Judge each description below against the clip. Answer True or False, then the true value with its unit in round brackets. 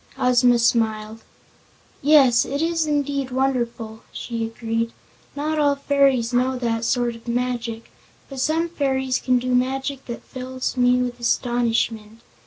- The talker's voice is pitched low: False (250 Hz)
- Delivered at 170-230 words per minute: False (135 wpm)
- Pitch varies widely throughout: False (2.6 semitones)